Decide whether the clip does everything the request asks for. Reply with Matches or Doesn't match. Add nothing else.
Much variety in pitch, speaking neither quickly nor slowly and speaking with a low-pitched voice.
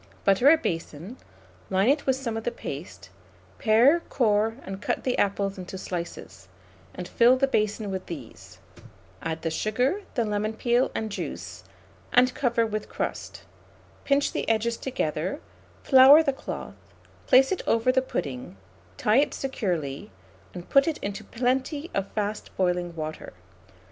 Doesn't match